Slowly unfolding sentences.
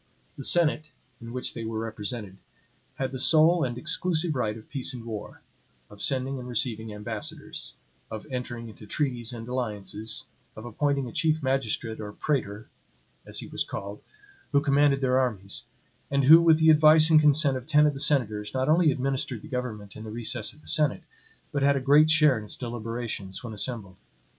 No: average, 185 wpm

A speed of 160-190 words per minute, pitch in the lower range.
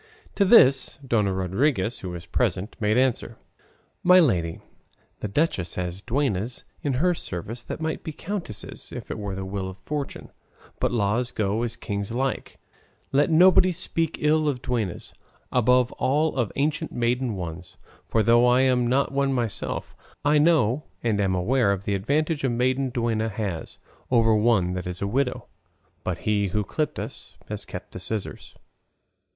Yes: average, 165 wpm; low, 120 Hz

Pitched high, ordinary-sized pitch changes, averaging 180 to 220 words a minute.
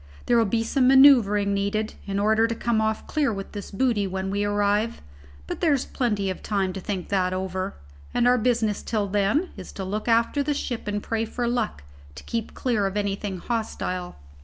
Yes: high, 210 Hz; average, 3.0 semitones; average, 195 wpm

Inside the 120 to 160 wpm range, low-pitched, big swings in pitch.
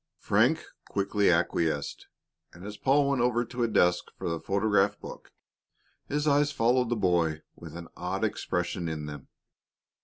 Yes: average, 155 wpm; low, 100 Hz; wide, 5.9 semitones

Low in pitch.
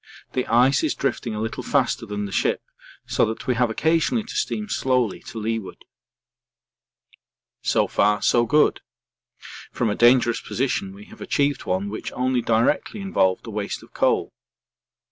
Yes: low, 120 Hz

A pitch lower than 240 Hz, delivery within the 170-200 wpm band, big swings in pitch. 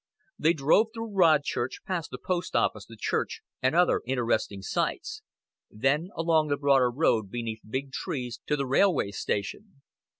No: medium, 140 Hz; average, 155 wpm; wide, 6.1 semitones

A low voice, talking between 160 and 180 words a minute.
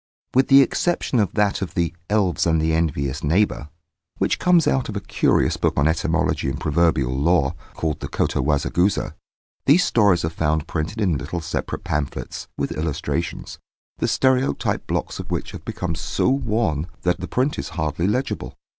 Yes: very low, 85 Hz; average, 170 wpm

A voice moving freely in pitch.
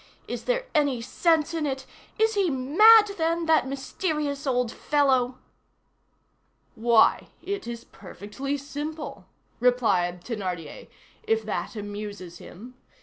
Yes: wide, 5.8 semitones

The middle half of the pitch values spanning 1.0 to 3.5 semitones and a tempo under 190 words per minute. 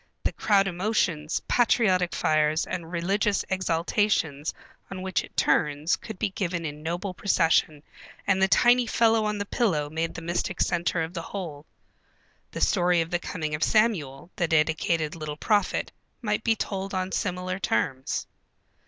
No: average, 3.9 semitones; average, 155 wpm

